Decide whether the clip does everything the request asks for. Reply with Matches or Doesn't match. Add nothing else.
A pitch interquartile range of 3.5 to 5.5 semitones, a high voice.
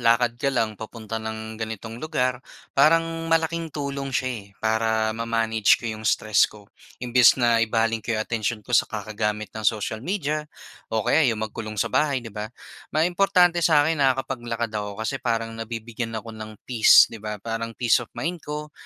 Doesn't match